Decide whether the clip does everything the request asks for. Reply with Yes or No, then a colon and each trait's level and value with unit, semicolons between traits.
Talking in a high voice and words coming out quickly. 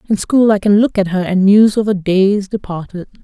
Yes: high, 200 Hz; fast, 225 wpm